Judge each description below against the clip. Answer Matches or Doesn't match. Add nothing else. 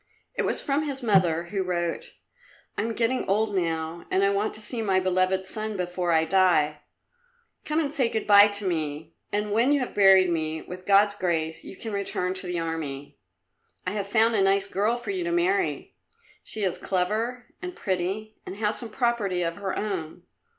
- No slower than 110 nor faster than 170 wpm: Doesn't match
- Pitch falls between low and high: Doesn't match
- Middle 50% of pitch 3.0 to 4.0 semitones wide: Matches